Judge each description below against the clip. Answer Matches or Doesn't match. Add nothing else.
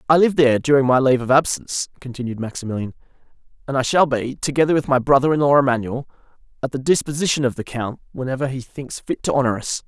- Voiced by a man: Matches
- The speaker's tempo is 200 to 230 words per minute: Matches